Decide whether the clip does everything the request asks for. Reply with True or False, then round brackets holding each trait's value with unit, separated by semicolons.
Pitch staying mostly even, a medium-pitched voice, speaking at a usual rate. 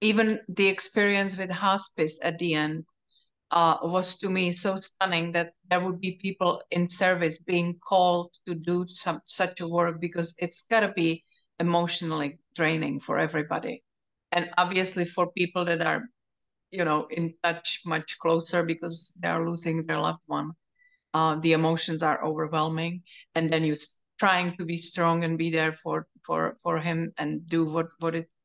True (1.7 semitones; 170 Hz; 170 wpm)